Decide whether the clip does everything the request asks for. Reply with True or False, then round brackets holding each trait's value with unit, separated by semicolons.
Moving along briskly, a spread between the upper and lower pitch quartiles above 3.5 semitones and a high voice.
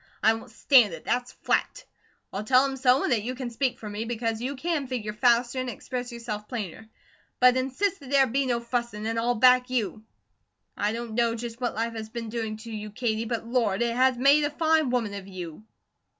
False (215 wpm; 2.7 semitones; 235 Hz)